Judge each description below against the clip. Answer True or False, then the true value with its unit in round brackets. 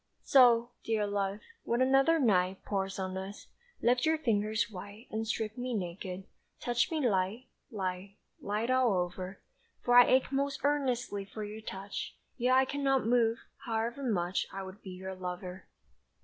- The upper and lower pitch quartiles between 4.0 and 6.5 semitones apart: True (4.4 semitones)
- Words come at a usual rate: True (160 wpm)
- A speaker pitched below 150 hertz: False (215 Hz)